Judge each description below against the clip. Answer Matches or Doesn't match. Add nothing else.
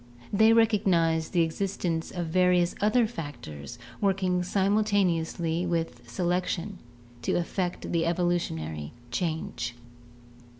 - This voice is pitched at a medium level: Matches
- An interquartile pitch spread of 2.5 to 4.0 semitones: Matches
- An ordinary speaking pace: Doesn't match